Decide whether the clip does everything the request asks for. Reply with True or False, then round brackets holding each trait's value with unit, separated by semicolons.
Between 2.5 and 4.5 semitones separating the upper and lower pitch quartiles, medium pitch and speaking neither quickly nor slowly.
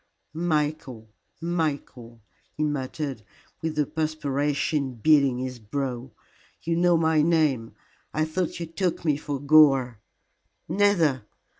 False (3.4 semitones; 150 Hz; 115 wpm)